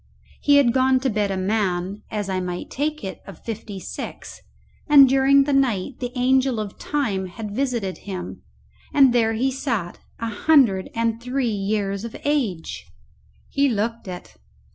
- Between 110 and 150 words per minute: No, average, 165 wpm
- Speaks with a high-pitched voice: Yes, high, 230 Hz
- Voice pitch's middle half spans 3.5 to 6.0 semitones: Yes, average, 5.1 semitones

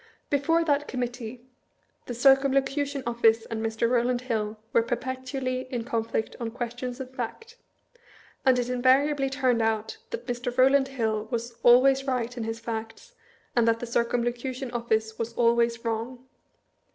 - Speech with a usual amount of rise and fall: No, narrow, 2.3 semitones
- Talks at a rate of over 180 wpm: No, average, 150 wpm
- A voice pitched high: Yes, high, 245 Hz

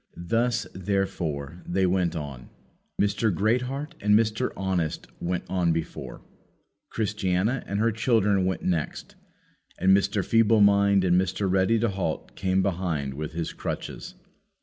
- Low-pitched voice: Yes, very low, 95 Hz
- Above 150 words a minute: No, slow, 135 wpm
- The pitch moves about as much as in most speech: Yes, average, 3.2 semitones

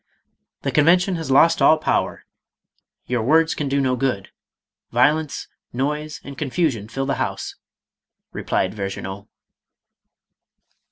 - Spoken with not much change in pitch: No, average, 4.3 semitones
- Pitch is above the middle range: No, medium, 140 Hz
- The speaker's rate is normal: No, slow, 130 wpm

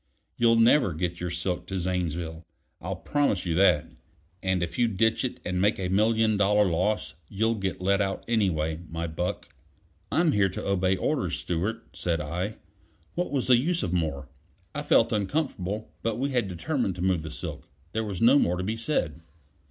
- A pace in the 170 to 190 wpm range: Yes, average, 185 wpm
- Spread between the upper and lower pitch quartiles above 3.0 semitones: Yes, average, 4.3 semitones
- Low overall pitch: Yes, very low, 95 Hz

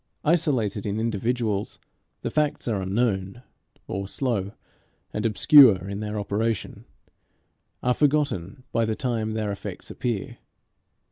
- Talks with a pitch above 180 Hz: No, low, 110 Hz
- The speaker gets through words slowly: Yes, slow, 120 wpm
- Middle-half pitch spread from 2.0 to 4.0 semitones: Yes, average, 3.6 semitones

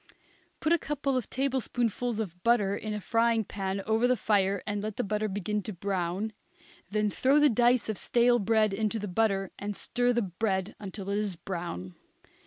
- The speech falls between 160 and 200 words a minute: Yes, average, 190 wpm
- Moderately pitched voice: No, high, 210 Hz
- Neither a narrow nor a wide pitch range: Yes, average, 3.2 semitones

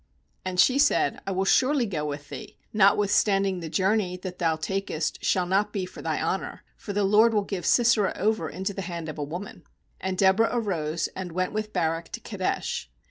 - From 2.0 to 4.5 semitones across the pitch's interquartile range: Yes, average, 3.1 semitones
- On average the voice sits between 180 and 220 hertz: Yes, high, 190 Hz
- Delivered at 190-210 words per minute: Yes, average, 195 wpm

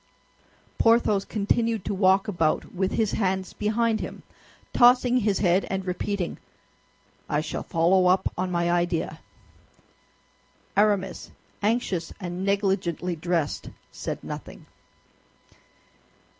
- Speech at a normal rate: No, slow, 105 wpm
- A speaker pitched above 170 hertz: Yes, high, 190 Hz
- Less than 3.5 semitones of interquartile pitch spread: Yes, average, 3.0 semitones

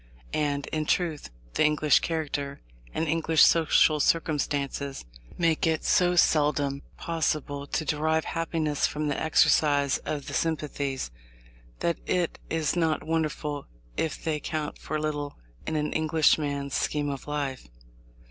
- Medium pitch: Yes, medium, 150 Hz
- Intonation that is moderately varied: No, narrow, 1.9 semitones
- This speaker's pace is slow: Yes, slow, 130 wpm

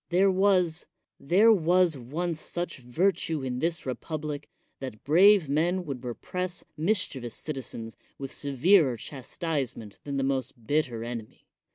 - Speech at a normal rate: Yes, average, 145 wpm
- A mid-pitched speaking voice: Yes, medium, 150 Hz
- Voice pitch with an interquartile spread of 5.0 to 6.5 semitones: Yes, average, 5.3 semitones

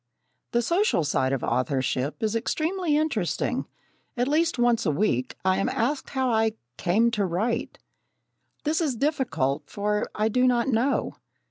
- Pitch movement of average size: No, wide, 6.7 semitones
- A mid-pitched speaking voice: No, high, 230 Hz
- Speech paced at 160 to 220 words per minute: No, average, 150 wpm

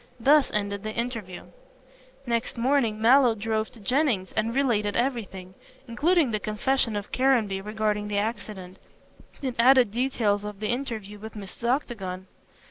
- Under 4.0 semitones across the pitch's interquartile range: Yes, average, 3.3 semitones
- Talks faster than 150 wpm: No, average, 140 wpm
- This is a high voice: Yes, high, 220 Hz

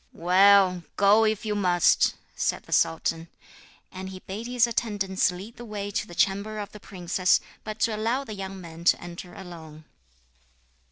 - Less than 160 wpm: No, average, 170 wpm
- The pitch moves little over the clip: No, average, 3.1 semitones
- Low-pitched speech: No, high, 195 Hz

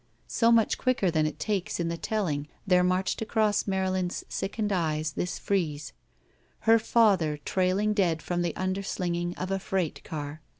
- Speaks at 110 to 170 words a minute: Yes, average, 160 wpm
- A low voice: No, medium, 185 Hz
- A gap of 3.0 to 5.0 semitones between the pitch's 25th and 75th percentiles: Yes, average, 3.7 semitones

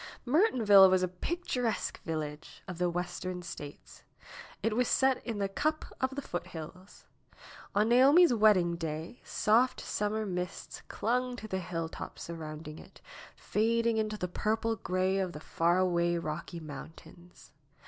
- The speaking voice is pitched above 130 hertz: Yes, medium, 185 Hz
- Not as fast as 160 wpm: Yes, average, 140 wpm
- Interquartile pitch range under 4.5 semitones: No, average, 4.8 semitones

